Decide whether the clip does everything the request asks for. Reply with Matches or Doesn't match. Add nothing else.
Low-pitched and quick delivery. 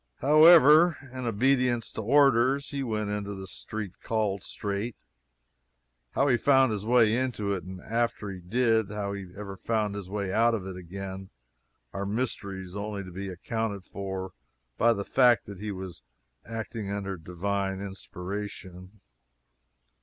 Doesn't match